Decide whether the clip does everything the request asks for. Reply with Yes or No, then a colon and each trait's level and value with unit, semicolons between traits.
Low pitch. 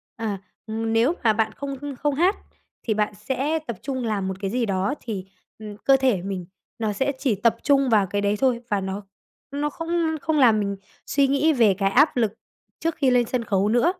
No: high, 230 Hz